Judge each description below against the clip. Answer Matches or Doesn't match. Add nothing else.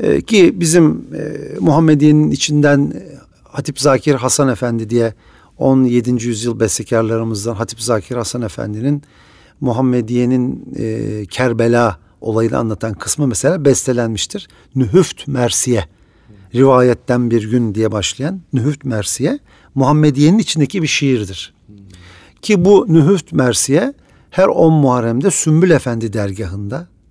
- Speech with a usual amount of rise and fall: Matches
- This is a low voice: Matches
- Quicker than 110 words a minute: Doesn't match